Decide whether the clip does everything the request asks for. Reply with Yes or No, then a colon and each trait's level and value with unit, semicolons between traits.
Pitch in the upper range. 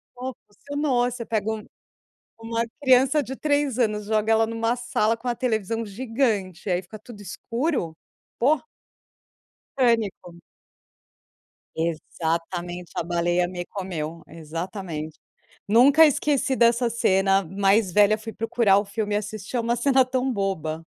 Yes: high, 220 Hz